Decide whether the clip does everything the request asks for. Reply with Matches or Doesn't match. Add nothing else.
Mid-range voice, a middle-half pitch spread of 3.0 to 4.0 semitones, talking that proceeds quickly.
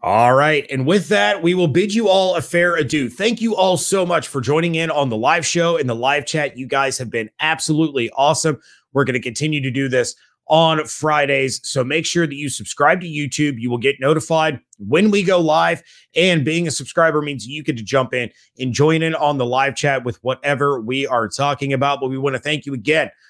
Matches